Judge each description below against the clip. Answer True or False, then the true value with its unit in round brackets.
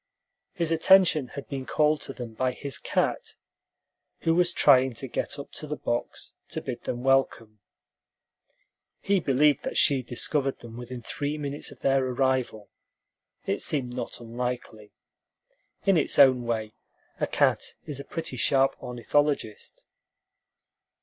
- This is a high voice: False (135 Hz)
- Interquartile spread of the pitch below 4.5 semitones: True (3.3 semitones)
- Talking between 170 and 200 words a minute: False (145 wpm)